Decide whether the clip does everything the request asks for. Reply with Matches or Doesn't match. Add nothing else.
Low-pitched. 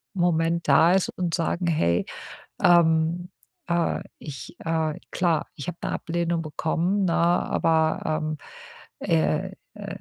Doesn't match